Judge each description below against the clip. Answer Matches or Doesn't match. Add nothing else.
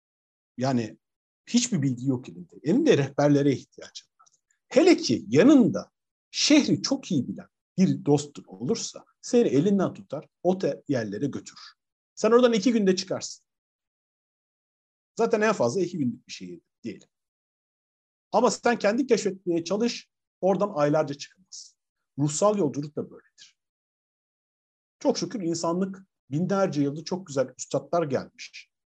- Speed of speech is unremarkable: Matches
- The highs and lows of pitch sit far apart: Matches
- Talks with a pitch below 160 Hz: Doesn't match